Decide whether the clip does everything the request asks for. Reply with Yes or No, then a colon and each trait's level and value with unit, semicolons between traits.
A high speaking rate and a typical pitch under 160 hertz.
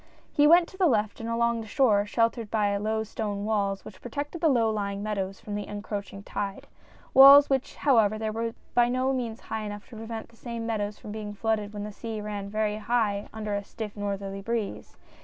No: fast, 215 wpm; high, 215 Hz